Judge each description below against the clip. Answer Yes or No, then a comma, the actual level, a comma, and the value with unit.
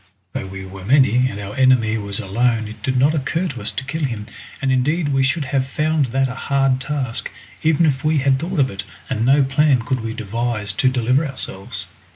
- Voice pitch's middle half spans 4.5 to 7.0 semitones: No, average, 3.6 semitones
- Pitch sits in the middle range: No, low, 130 Hz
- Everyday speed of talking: No, fast, 215 wpm